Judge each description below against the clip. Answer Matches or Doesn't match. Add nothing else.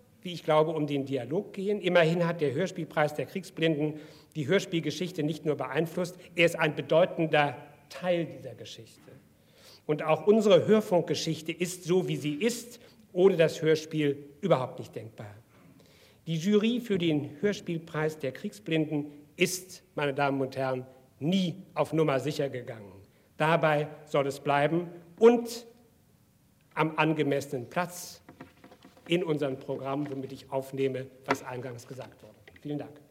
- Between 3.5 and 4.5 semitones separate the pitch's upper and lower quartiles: Matches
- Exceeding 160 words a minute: Doesn't match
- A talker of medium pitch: Matches